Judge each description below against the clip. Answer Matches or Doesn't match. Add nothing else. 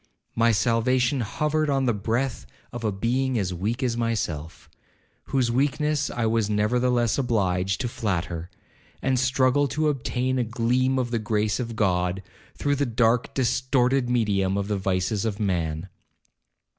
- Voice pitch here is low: Matches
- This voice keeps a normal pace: Matches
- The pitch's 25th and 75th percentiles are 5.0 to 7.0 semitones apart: Doesn't match